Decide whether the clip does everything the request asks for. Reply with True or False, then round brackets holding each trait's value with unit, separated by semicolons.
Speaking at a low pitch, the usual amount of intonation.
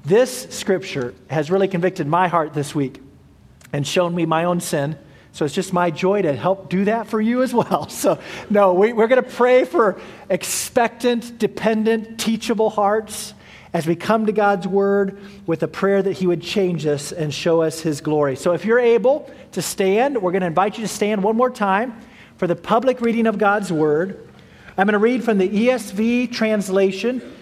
False (195 Hz; 4.4 semitones)